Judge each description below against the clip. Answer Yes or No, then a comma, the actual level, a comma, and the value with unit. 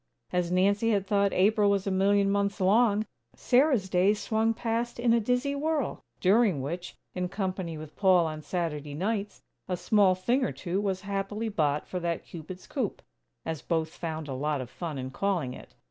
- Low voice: No, high, 195 Hz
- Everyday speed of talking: Yes, average, 185 wpm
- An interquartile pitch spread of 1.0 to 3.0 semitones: No, average, 3.9 semitones